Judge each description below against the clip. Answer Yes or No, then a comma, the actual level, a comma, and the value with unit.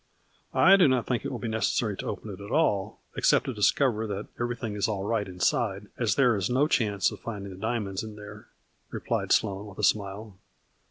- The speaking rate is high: Yes, fast, 210 wpm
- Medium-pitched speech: No, low, 105 Hz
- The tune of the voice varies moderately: Yes, average, 3.0 semitones